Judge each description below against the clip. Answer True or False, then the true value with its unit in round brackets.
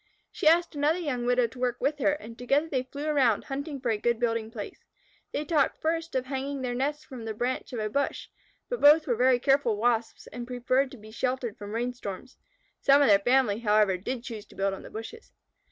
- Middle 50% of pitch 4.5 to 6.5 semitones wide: False (3.7 semitones)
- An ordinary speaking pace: False (220 wpm)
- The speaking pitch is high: True (250 Hz)